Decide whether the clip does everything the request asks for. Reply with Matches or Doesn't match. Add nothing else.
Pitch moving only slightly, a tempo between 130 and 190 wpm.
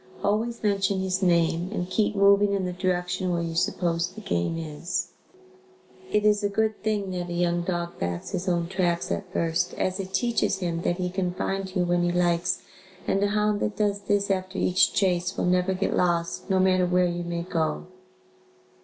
Doesn't match